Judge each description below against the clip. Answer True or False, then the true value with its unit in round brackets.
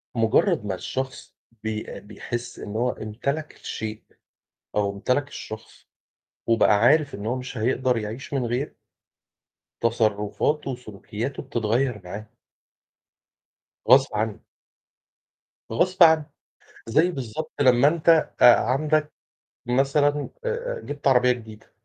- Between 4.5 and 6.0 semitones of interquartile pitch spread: True (4.8 semitones)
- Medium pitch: False (125 Hz)